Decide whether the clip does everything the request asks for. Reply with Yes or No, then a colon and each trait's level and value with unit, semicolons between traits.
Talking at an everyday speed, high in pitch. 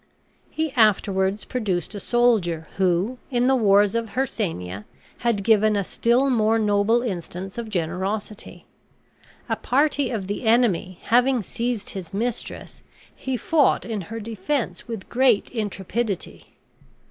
No: slow, 130 wpm; high, 220 Hz